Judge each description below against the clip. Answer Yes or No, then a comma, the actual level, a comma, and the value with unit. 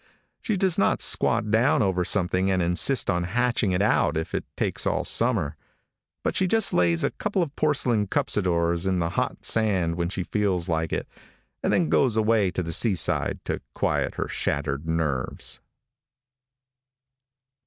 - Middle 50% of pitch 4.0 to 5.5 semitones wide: Yes, average, 5.2 semitones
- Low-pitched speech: Yes, very low, 95 Hz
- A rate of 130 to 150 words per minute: No, average, 165 wpm